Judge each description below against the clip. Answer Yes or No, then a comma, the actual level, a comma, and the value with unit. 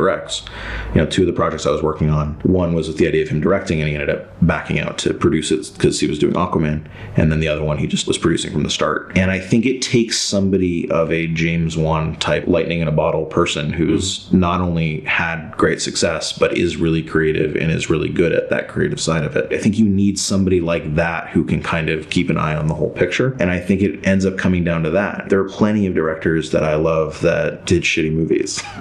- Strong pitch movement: No, average, 3.2 semitones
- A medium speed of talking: No, fast, 250 wpm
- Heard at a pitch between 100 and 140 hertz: No, very low, 85 Hz